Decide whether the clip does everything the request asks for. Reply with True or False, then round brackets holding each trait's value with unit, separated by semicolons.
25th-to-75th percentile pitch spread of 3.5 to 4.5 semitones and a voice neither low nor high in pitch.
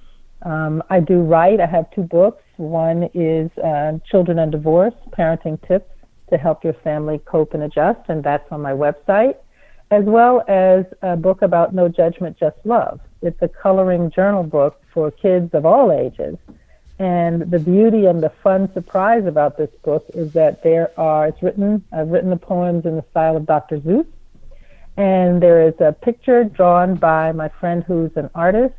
False (3.0 semitones; 170 Hz)